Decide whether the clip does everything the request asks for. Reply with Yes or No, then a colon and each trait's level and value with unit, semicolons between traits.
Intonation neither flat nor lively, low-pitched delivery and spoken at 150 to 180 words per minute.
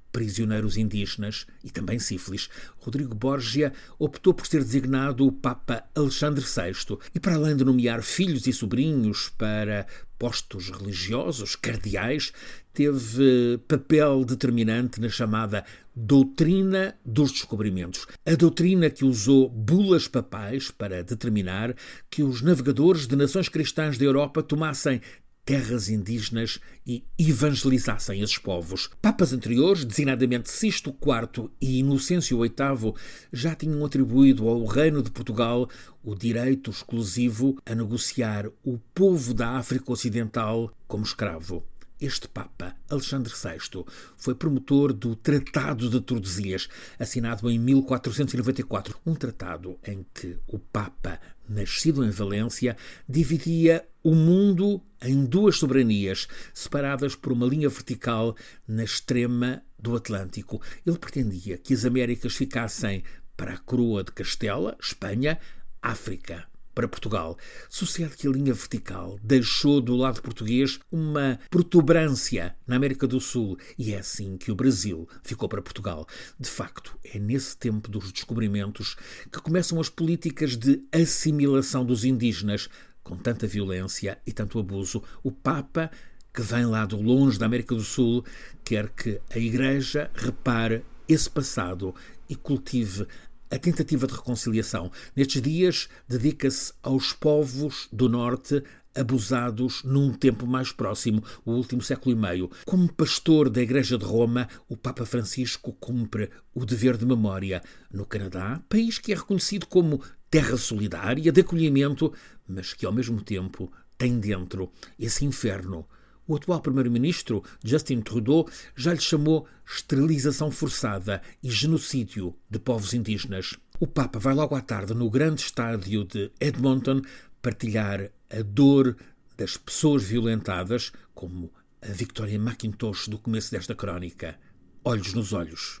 No: average, 4.4 semitones; low, 125 Hz; average, 135 wpm